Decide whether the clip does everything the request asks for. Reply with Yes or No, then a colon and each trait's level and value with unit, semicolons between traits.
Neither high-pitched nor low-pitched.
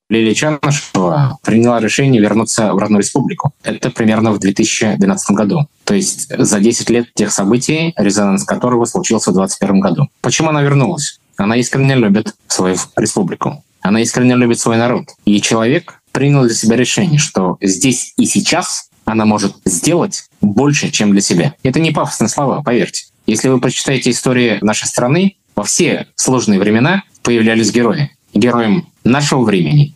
No: low, 120 Hz